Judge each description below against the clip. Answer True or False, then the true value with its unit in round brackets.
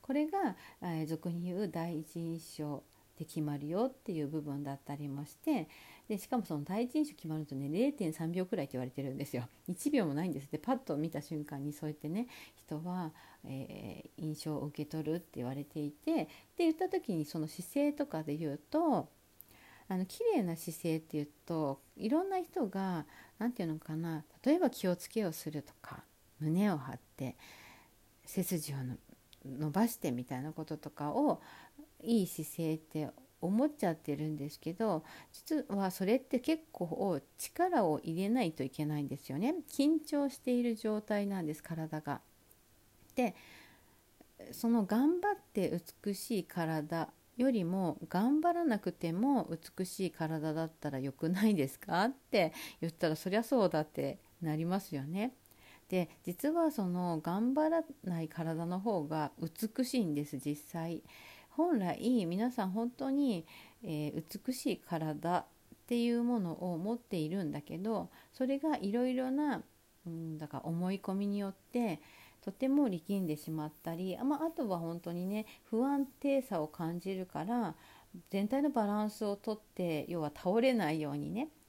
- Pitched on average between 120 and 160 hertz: False (175 Hz)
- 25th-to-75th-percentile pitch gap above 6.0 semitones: True (7.4 semitones)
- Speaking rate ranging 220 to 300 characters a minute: True (295 characters per minute)